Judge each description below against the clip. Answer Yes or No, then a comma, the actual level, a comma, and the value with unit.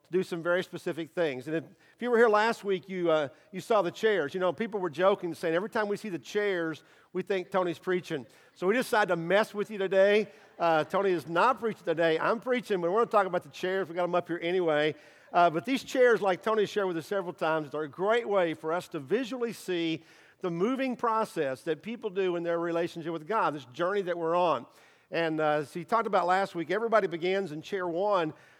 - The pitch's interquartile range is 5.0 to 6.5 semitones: No, average, 3.6 semitones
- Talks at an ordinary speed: No, fast, 240 wpm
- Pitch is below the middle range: No, medium, 180 Hz